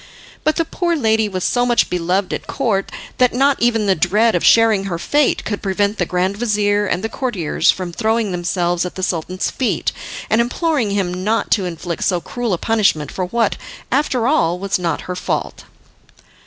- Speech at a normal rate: Yes, average, 190 wpm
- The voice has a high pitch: Yes, high, 205 Hz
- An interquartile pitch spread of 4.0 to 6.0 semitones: Yes, average, 4.5 semitones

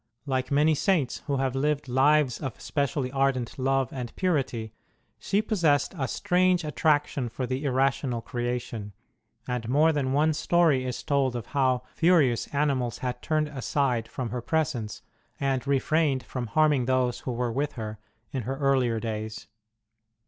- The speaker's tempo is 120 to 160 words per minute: Yes, average, 155 wpm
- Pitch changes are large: No, average, 3.2 semitones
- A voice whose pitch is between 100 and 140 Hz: Yes, low, 135 Hz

